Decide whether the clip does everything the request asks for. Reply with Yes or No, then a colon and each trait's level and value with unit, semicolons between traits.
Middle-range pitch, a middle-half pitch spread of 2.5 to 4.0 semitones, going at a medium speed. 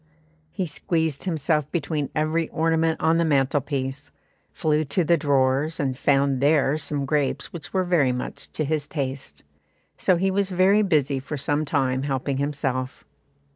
Yes: medium, 150 Hz; average, 2.9 semitones; average, 150 wpm